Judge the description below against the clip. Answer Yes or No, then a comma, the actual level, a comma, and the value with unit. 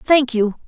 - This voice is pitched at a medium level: No, very high, 250 Hz